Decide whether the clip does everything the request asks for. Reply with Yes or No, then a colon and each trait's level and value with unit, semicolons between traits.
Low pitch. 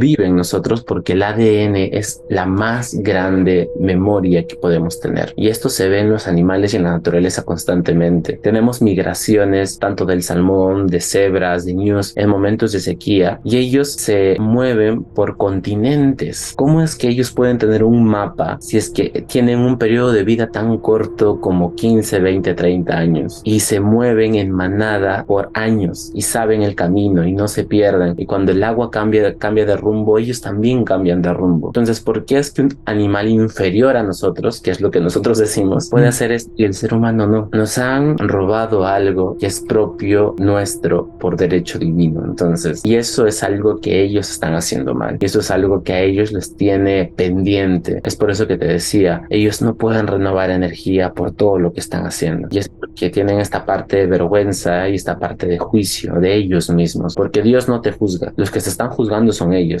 Yes: low, 100 Hz